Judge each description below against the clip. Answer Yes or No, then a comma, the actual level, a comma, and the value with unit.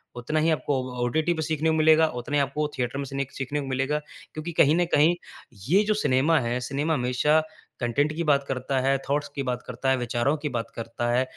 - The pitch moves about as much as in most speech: Yes, average, 3.4 semitones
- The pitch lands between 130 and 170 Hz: Yes, medium, 140 Hz